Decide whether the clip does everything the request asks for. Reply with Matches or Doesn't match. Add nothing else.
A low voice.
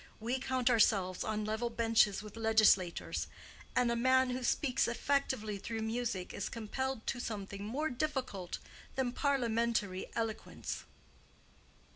Doesn't match